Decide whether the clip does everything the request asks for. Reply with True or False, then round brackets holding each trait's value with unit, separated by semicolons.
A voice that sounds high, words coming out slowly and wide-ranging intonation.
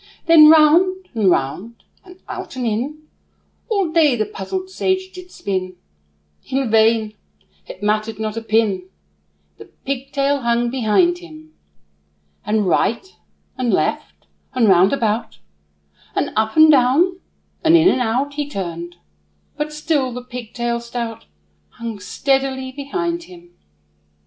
True (250 Hz; 130 wpm; 6.2 semitones)